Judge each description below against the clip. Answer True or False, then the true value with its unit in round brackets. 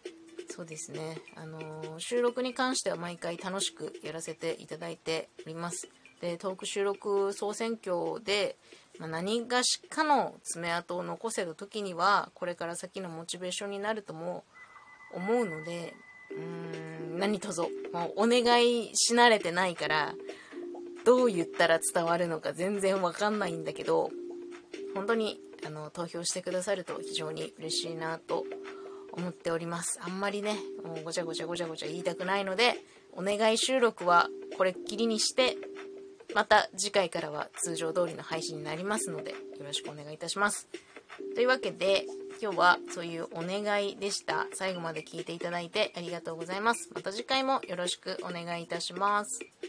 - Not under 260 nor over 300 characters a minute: False (345 characters per minute)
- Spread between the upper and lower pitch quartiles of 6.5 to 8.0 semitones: False (5.7 semitones)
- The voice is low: False (190 Hz)